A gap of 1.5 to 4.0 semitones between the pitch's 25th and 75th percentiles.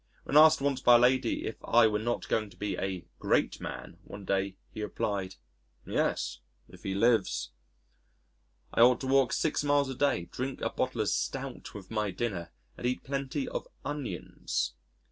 No: average, 5.2 semitones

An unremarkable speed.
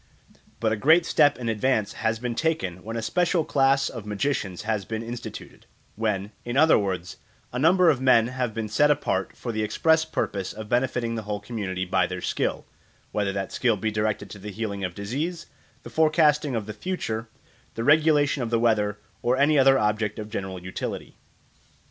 Yes: average, 190 wpm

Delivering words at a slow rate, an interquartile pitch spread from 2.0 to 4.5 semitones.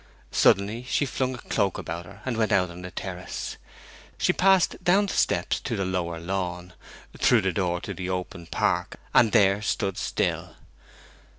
No: average, 175 wpm; average, 4.0 semitones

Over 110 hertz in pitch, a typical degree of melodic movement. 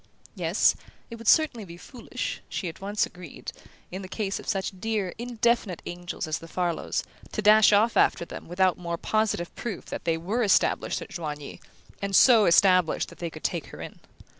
Yes: high, 190 Hz; average, 4.0 semitones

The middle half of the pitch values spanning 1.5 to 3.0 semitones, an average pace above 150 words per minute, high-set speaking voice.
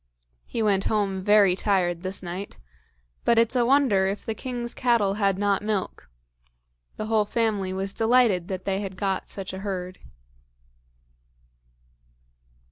No: narrow, 2.6 semitones; average, 140 wpm; high, 200 Hz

